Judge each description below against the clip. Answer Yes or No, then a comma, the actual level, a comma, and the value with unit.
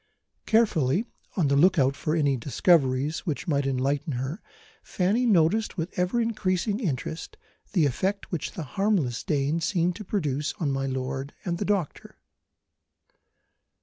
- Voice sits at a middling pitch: Yes, medium, 160 Hz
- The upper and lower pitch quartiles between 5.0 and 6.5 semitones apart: Yes, wide, 5.6 semitones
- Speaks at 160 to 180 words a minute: No, average, 145 wpm